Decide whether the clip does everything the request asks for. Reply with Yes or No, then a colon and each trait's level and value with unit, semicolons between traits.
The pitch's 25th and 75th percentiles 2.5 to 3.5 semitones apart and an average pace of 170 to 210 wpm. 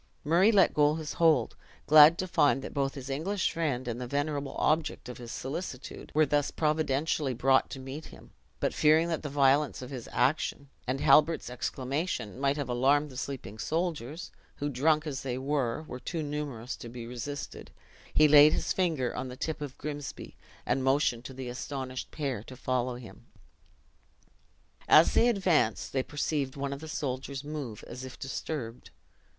Yes: average, 3.1 semitones; average, 175 wpm